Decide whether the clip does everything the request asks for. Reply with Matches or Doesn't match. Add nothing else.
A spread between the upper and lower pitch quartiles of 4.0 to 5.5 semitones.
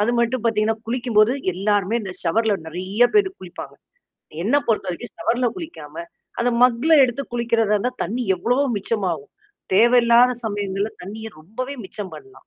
Doesn't match